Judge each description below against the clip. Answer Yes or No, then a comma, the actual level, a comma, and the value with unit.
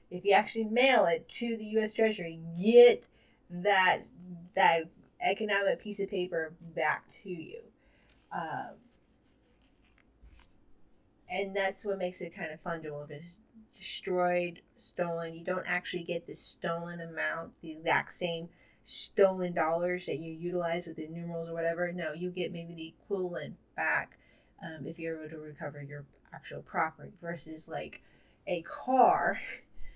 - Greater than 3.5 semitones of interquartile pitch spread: No, average, 2.9 semitones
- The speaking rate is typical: Yes, average, 145 wpm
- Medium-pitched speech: Yes, medium, 175 Hz